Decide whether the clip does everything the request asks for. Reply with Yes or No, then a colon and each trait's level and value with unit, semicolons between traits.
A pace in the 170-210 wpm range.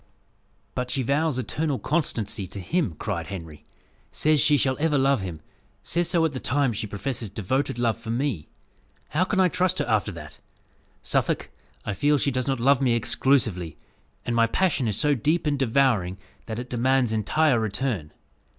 Yes: average, 180 wpm